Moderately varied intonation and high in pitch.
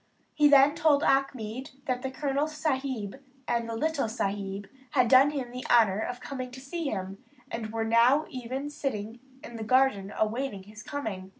Yes: average, 4.0 semitones; very high, 250 Hz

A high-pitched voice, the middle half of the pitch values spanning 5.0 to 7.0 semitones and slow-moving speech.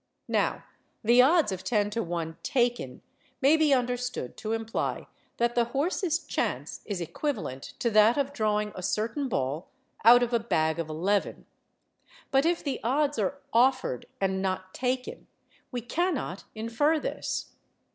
No: high, 235 Hz; wide, 5.5 semitones; average, 150 wpm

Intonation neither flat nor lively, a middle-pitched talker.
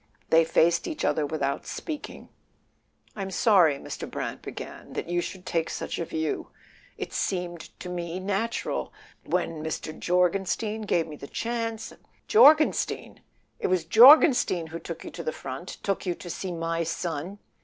Yes: average, 3.4 semitones; medium, 175 Hz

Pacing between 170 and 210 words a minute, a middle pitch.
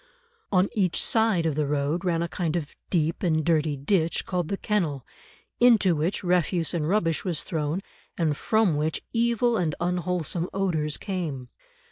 No: average, 160 wpm; medium, 170 Hz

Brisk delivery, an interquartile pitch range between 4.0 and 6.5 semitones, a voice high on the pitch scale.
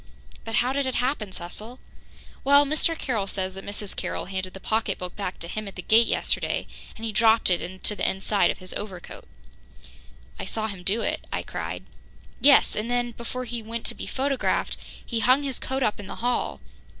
Yes: fast, 210 wpm; average, 4.4 semitones; high, 220 Hz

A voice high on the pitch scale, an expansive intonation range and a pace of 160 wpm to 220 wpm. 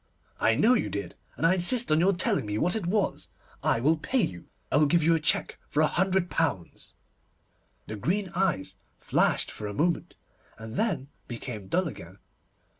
No: medium, 165 Hz; wide, 8.7 semitones; average, 190 wpm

